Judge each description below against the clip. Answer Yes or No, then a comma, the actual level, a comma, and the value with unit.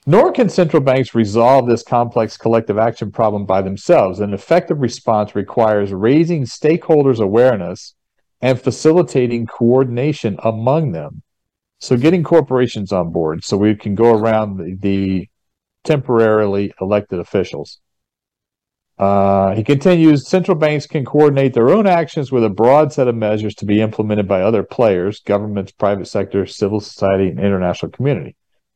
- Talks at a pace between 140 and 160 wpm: Yes, average, 145 wpm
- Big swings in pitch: Yes, wide, 5.9 semitones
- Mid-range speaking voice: No, low, 115 Hz